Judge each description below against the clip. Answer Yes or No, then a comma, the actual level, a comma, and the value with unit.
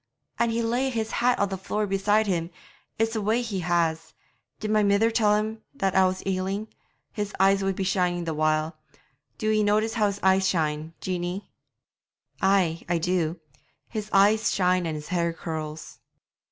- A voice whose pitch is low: No, high, 195 Hz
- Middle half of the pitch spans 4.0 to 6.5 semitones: No, average, 3.5 semitones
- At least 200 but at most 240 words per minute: No, average, 180 wpm